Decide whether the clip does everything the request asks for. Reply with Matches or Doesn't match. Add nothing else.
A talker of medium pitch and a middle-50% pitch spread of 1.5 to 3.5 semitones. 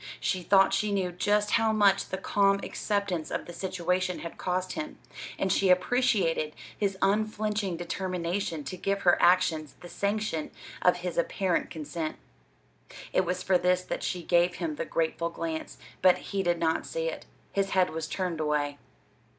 Matches